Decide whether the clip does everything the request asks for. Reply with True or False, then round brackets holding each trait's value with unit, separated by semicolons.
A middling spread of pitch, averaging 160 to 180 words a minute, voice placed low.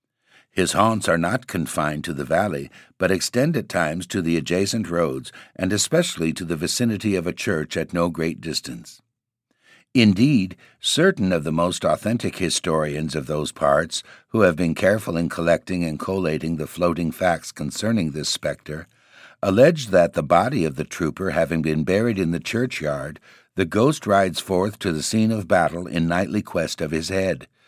True (4.2 semitones; 175 wpm; 90 Hz)